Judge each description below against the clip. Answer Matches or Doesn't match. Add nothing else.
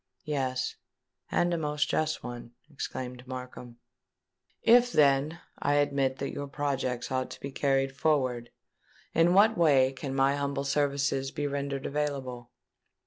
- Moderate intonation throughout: Doesn't match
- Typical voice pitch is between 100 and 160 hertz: Matches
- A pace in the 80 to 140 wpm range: Matches